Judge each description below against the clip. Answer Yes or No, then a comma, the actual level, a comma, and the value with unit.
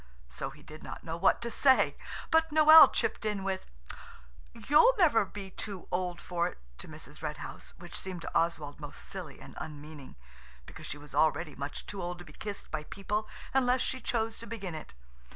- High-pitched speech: No, medium, 180 Hz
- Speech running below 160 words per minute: No, average, 190 wpm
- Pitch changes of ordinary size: No, wide, 6.3 semitones